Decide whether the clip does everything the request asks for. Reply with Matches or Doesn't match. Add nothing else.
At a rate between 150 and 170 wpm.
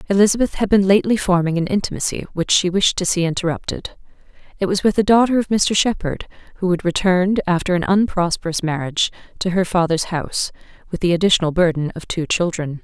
Doesn't match